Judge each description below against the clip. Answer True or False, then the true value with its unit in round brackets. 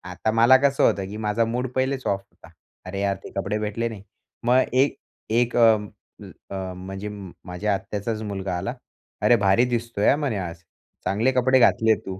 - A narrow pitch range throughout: False (3.7 semitones)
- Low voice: True (105 Hz)